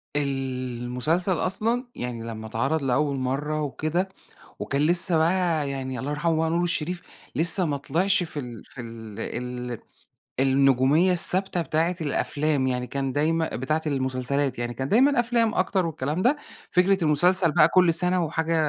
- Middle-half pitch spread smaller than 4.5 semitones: No, average, 4.9 semitones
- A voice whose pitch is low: No, medium, 150 Hz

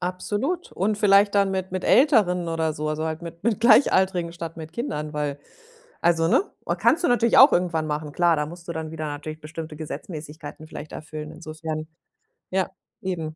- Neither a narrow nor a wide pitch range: Yes, average, 3.4 semitones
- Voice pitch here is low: No, medium, 165 Hz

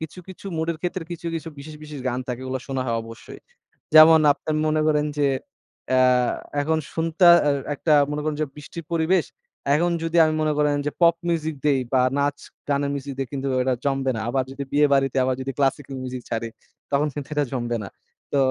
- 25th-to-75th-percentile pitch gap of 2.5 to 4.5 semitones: Yes, average, 2.9 semitones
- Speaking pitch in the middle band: Yes, medium, 145 Hz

